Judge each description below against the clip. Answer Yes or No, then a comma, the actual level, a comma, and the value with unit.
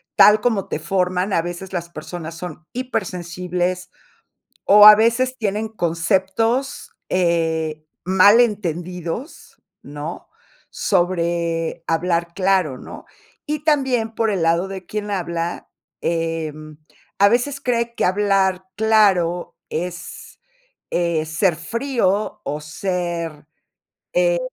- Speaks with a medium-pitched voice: Yes, medium, 180 Hz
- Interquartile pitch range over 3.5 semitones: Yes, average, 4.0 semitones